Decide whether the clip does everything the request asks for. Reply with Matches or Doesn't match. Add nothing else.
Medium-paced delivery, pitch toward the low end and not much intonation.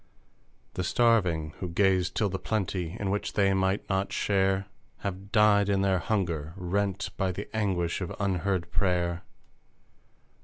Matches